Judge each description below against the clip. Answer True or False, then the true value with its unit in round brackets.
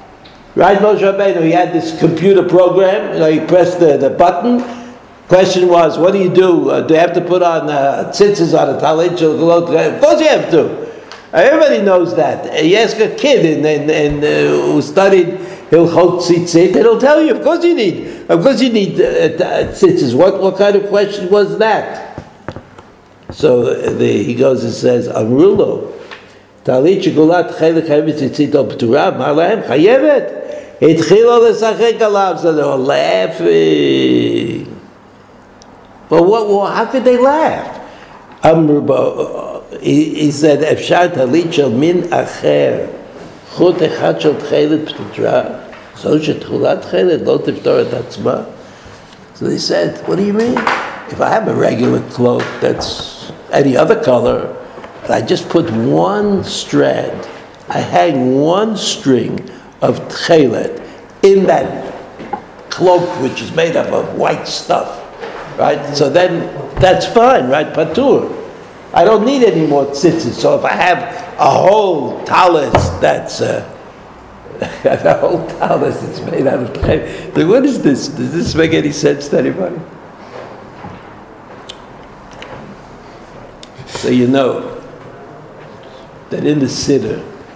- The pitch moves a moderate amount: False (7.2 semitones)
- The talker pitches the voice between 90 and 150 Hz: False (185 Hz)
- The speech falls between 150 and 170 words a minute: False (135 wpm)